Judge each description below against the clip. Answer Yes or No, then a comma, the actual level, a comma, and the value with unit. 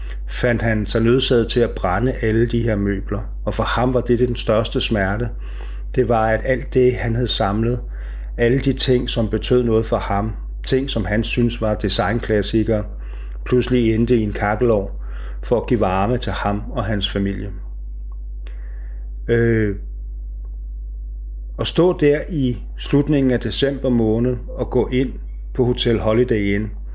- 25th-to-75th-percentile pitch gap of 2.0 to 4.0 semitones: No, average, 4.6 semitones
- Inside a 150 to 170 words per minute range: Yes, average, 160 wpm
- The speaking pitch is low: Yes, low, 110 Hz